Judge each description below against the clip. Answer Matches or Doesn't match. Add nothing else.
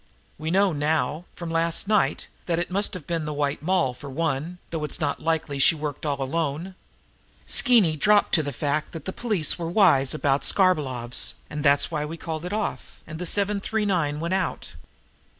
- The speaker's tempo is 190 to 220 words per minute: Matches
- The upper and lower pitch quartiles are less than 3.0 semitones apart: Doesn't match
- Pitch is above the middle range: Doesn't match